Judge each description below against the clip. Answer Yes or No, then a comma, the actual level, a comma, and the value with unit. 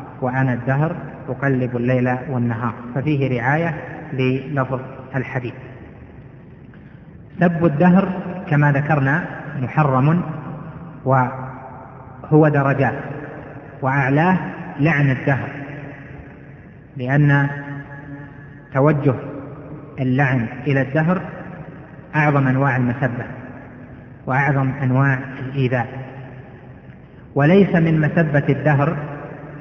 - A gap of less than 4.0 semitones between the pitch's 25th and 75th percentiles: Yes, narrow, 2.6 semitones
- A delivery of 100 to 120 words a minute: No, average, 70 wpm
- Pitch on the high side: No, medium, 140 Hz